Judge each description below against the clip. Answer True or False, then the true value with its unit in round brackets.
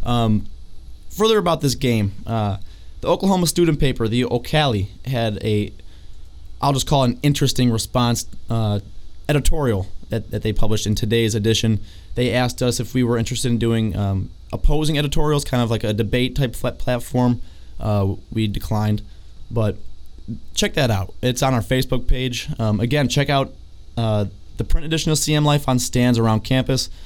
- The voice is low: True (115 Hz)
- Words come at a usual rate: True (170 wpm)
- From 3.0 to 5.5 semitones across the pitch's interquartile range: True (3.9 semitones)